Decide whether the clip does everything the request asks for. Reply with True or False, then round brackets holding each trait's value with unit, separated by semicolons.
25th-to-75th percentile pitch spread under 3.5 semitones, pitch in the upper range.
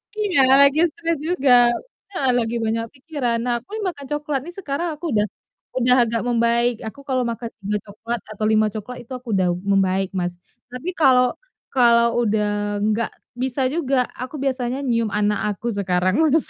False (4.2 semitones; 240 Hz)